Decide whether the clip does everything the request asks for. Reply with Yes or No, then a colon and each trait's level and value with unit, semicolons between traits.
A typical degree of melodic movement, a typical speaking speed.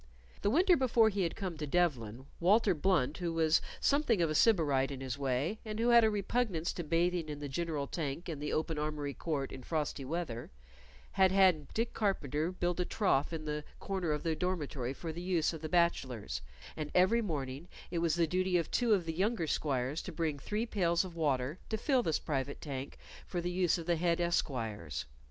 No: average, 4.3 semitones; fast, 210 wpm